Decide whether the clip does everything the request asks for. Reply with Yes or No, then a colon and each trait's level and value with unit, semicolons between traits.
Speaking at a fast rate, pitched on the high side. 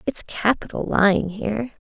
No: slow, 130 wpm; high, 210 Hz